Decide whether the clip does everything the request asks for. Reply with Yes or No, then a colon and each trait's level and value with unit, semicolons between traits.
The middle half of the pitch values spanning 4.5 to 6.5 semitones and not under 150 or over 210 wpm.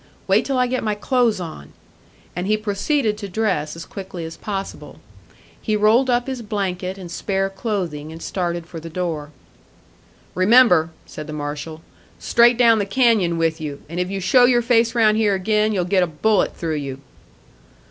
Yes: average, 5.0 semitones; average, 180 wpm